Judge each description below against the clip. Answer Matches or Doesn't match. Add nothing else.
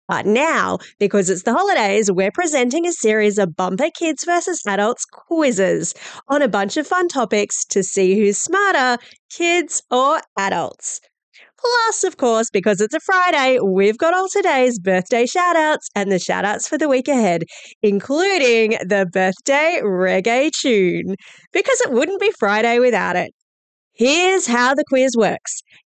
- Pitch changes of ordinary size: Doesn't match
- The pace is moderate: Matches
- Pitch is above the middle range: Matches